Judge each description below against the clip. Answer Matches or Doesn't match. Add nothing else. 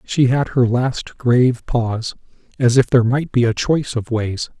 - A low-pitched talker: Matches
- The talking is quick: Doesn't match